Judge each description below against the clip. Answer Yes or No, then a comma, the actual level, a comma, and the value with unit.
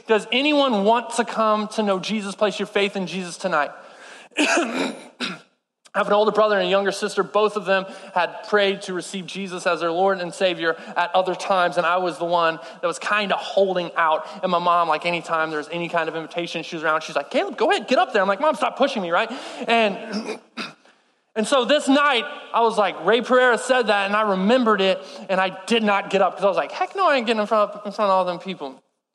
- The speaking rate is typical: No, fast, 245 wpm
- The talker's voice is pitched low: No, high, 195 Hz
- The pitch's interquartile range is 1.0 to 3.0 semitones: No, average, 3.7 semitones